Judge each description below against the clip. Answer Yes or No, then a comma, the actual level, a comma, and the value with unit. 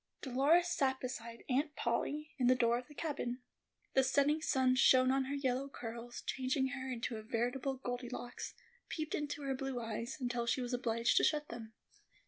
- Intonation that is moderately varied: No, narrow, 2.3 semitones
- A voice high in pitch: Yes, very high, 255 Hz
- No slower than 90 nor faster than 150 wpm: No, average, 180 wpm